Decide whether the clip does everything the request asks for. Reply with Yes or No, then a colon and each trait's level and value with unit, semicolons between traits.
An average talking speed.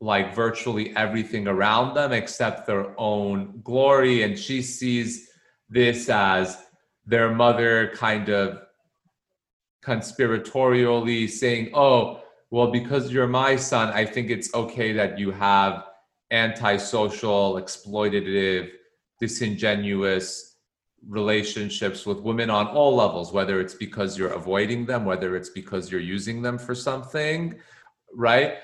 No: slow, 120 wpm